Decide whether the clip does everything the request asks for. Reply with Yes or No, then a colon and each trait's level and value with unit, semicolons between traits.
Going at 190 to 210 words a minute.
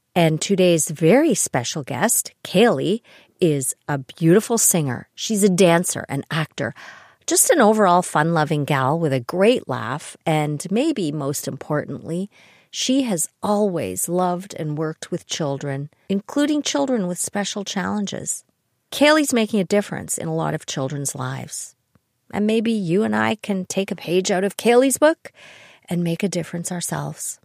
No: average, 150 wpm